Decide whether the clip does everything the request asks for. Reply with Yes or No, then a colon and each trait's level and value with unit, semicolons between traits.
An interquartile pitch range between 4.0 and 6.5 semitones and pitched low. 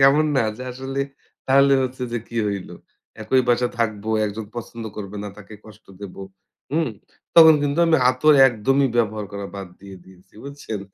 Yes: average, 4.7 semitones; low, 120 Hz